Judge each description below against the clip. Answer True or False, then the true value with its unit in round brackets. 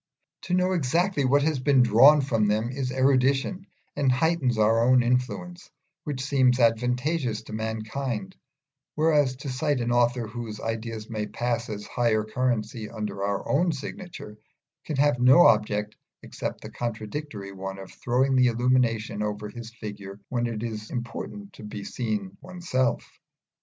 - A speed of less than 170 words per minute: True (150 wpm)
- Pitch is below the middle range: True (120 Hz)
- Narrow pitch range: False (4.0 semitones)